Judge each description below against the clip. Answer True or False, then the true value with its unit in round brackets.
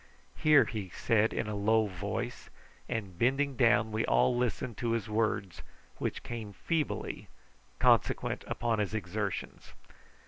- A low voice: True (110 Hz)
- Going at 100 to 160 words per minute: True (135 wpm)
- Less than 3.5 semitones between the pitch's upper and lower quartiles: True (2.6 semitones)